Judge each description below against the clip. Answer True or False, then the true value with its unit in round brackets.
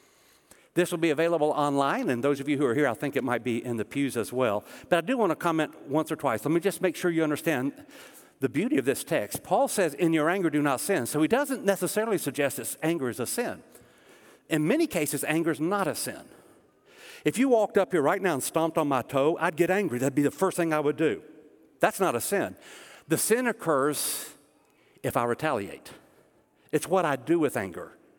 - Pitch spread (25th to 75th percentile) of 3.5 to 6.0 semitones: True (4.1 semitones)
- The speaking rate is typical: False (230 wpm)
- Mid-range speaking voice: True (155 Hz)